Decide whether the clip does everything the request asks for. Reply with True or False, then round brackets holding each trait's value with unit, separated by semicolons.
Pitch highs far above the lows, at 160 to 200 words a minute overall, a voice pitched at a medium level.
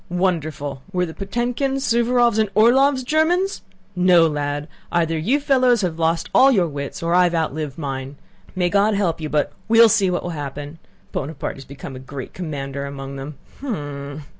True (7.8 semitones; 175 wpm; 170 Hz)